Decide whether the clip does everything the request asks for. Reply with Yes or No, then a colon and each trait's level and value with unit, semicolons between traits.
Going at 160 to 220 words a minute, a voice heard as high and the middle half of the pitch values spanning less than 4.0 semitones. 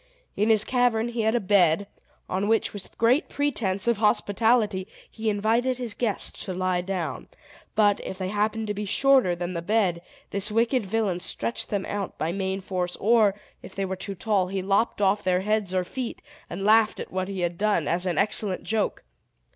Yes: average, 195 wpm; high, 205 Hz; average, 2.9 semitones